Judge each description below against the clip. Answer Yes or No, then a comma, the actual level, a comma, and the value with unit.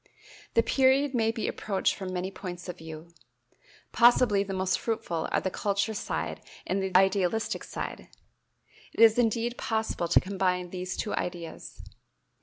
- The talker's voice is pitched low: No, high, 195 Hz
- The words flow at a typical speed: Yes, average, 150 wpm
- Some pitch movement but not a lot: Yes, average, 3.7 semitones